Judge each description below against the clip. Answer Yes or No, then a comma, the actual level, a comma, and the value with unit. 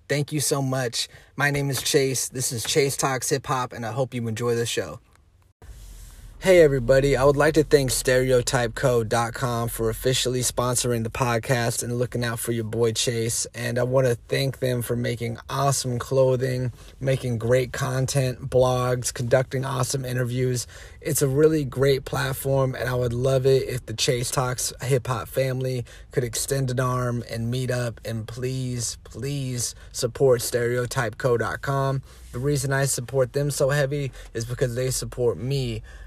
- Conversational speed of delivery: Yes, average, 165 wpm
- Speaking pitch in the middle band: No, low, 125 Hz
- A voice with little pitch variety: Yes, narrow, 2.1 semitones